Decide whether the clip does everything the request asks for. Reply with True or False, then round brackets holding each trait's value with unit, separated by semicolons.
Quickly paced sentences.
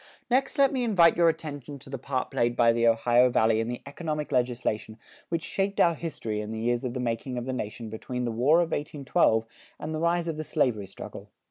True (225 wpm)